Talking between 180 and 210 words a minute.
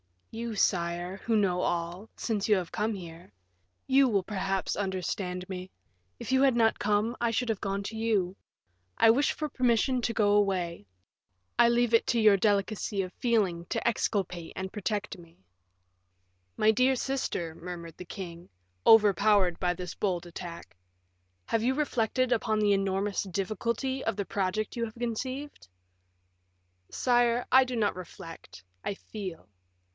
No: average, 155 wpm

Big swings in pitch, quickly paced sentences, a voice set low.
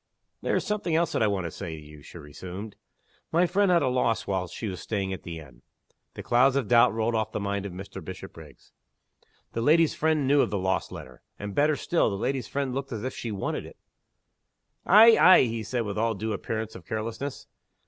Yes: wide, 6.2 semitones; fast, 220 wpm; low, 110 Hz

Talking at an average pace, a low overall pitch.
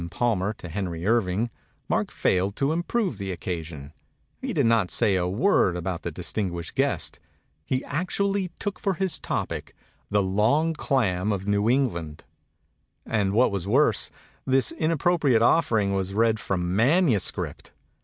Yes: average, 150 wpm; low, 105 Hz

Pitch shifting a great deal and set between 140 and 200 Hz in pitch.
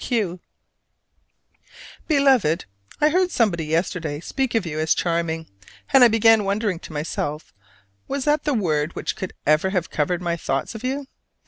Yes: wide, 7.2 semitones; medium, 185 Hz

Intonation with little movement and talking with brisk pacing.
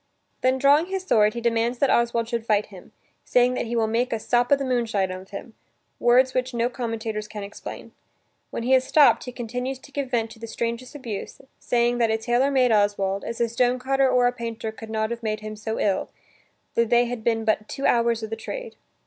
Yes: narrow, 2.3 semitones; fast, 230 wpm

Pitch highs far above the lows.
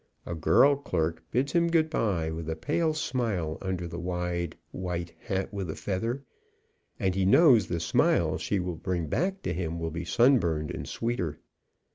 Yes: wide, 6.4 semitones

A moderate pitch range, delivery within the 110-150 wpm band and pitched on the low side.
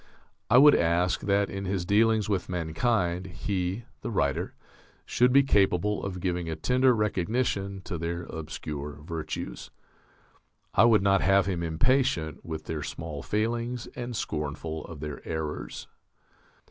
Yes: average, 4.9 semitones; average, 140 wpm; very low, 95 Hz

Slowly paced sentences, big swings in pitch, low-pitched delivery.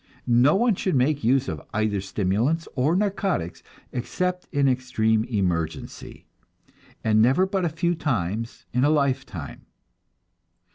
Yes: slow, 130 wpm; wide, 7.2 semitones; low, 130 Hz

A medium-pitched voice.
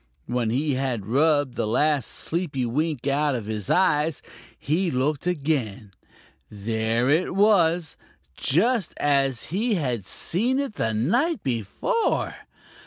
Yes: medium, 145 Hz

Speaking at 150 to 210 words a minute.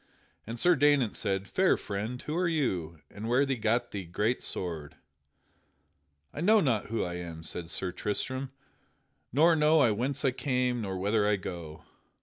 Yes: average, 165 wpm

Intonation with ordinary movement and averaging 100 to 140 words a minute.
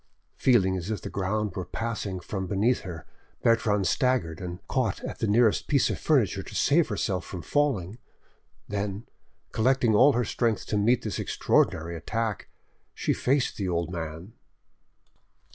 No: average, 4.4 semitones; average, 155 wpm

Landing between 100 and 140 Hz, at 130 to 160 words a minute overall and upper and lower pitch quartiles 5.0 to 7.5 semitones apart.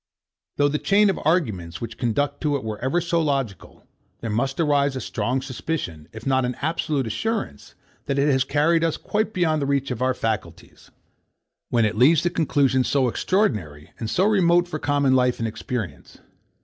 No: low, 135 Hz; average, 185 wpm; wide, 5.5 semitones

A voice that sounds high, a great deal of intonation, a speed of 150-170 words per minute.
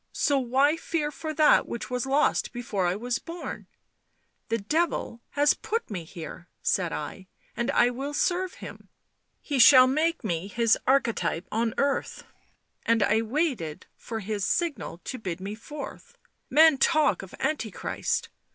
Yes: high, 245 Hz; wide, 6.3 semitones; average, 160 wpm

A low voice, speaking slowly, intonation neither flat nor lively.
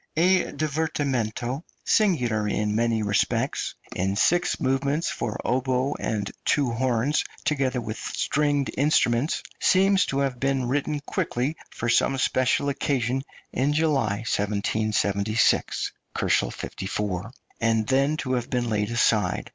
Yes: low, 125 Hz; slow, 125 wpm; average, 4.6 semitones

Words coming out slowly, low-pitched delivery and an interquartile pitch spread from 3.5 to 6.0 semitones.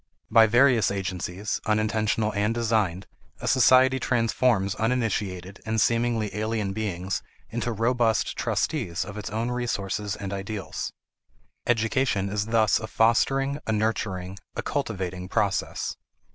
No: slow, 120 wpm; low, 110 Hz; average, 2.9 semitones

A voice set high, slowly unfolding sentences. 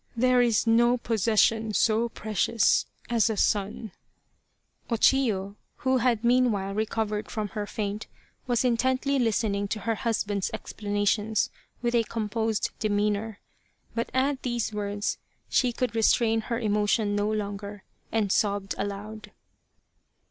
Yes: high, 220 Hz; slow, 130 wpm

